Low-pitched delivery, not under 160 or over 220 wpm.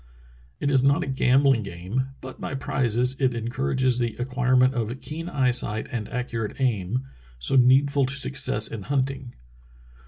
No: low, 130 Hz; average, 150 wpm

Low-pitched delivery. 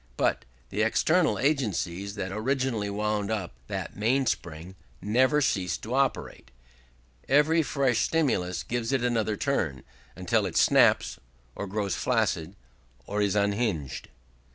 Yes: low, 110 Hz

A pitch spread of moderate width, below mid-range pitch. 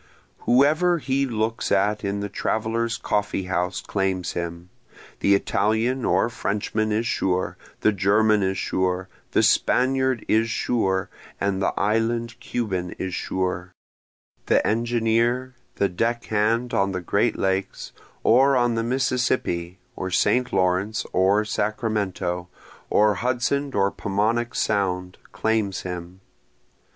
Yes: average, 3.8 semitones; low, 105 Hz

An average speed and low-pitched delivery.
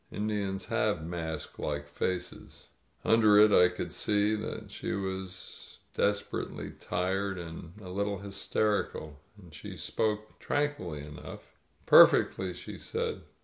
No: slow, 125 wpm; very low, 95 Hz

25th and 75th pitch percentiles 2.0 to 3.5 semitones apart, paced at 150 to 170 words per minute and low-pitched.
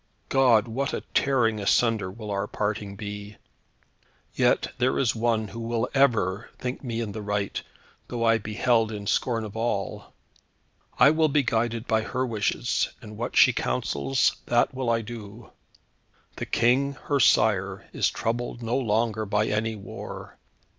Yes: narrow, 2.5 semitones; average, 160 wpm; low, 115 Hz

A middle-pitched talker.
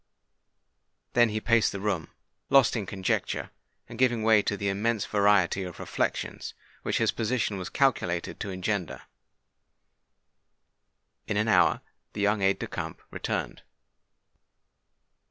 No: low, 105 Hz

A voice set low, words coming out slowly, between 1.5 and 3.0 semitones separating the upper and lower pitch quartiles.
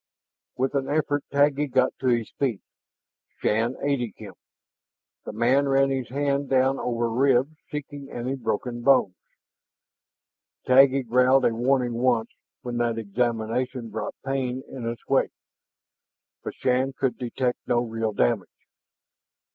Yes: low, 125 Hz; slow, 130 wpm; narrow, 2.5 semitones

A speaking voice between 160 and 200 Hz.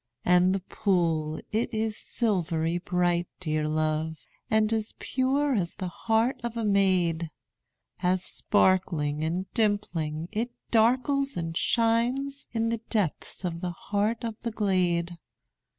Yes: high, 190 Hz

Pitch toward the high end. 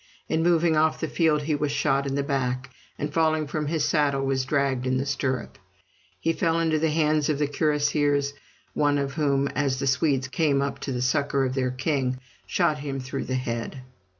No: medium, 140 Hz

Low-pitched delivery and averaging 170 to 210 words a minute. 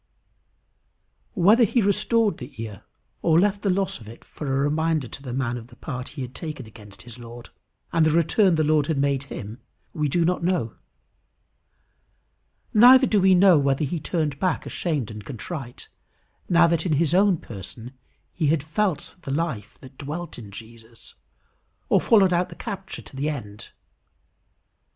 No: medium, 150 Hz; average, 175 wpm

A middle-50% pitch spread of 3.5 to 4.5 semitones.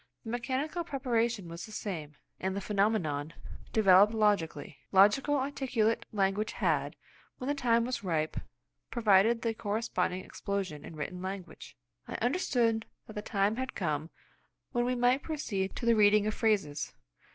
Yes: average, 4.1 semitones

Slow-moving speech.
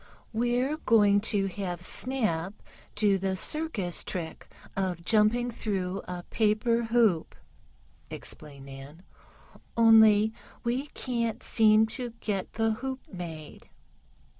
Yes: slow, 110 wpm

